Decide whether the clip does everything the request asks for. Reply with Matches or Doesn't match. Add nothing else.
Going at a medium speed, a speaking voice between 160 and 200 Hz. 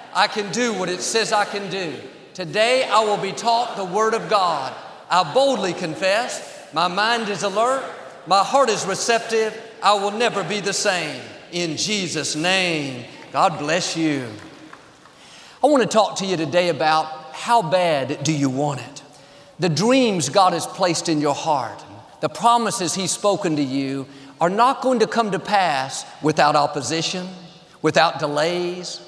Matches